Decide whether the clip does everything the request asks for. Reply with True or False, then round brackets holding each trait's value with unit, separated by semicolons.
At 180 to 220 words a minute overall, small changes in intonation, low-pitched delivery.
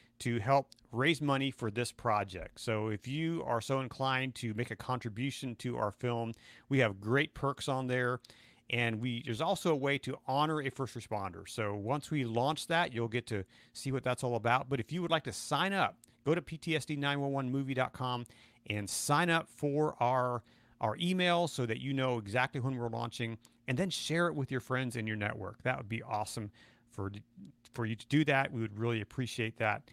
False (205 wpm; 3.3 semitones; 125 Hz)